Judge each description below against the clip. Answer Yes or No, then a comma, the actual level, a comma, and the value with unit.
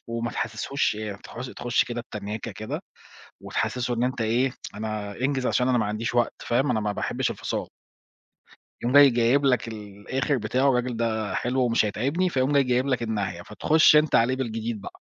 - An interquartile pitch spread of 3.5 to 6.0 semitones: No, average, 3.0 semitones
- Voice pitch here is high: No, low, 120 Hz